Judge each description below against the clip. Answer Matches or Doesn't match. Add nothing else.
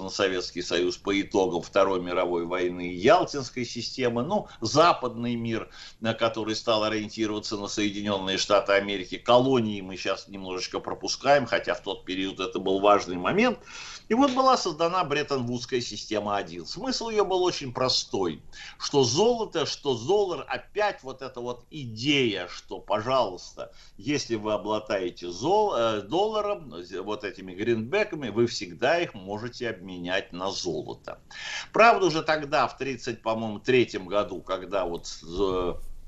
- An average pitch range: Doesn't match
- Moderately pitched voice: Doesn't match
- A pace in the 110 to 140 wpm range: Matches